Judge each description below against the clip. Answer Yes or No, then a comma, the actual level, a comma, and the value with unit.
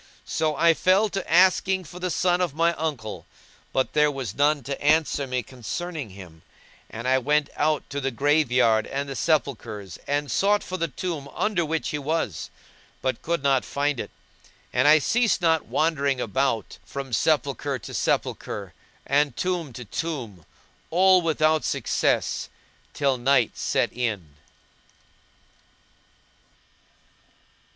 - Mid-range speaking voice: Yes, medium, 145 Hz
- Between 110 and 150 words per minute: Yes, average, 145 wpm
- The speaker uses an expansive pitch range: No, average, 4.2 semitones